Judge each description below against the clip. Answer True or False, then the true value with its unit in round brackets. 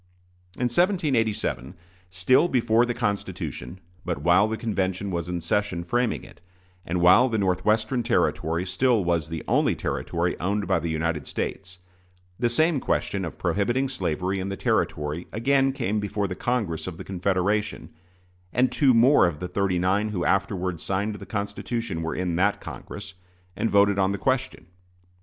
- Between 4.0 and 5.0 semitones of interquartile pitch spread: True (4.5 semitones)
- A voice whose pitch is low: True (100 Hz)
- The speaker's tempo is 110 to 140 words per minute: False (160 wpm)